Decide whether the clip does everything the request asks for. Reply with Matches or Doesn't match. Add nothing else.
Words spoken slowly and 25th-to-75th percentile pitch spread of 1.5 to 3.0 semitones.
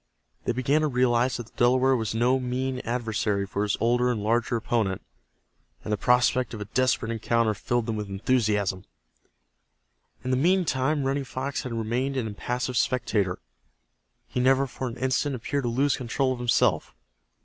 Doesn't match